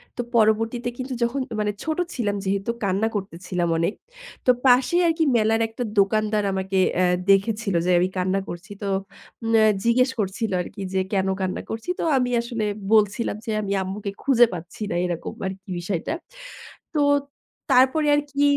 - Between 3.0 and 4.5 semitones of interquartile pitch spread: Yes, average, 3.9 semitones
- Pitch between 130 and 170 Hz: No, high, 215 Hz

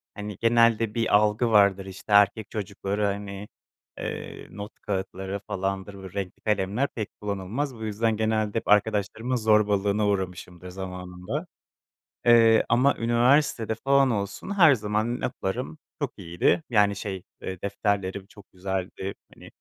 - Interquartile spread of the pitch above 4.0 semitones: No, average, 2.8 semitones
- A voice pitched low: Yes, low, 105 Hz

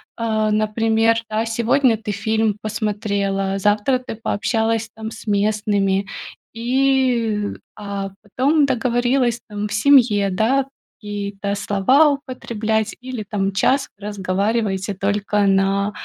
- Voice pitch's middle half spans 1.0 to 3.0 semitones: Yes, narrow, 2.5 semitones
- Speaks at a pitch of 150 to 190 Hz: No, high, 215 Hz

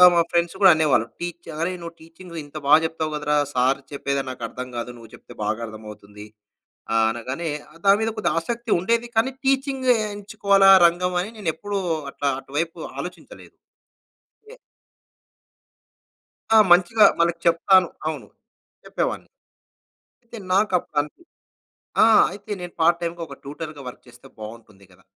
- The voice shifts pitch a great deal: Yes, wide, 5.8 semitones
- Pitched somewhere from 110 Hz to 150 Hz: No, medium, 170 Hz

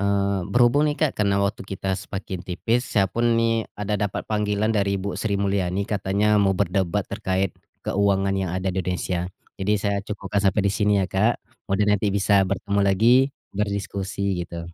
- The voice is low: Yes, low, 100 Hz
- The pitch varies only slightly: Yes, narrow, 1.4 semitones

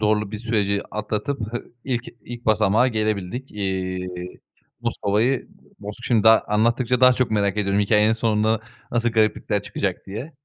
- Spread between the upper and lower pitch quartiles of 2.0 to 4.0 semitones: Yes, narrow, 2.5 semitones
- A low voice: Yes, low, 110 Hz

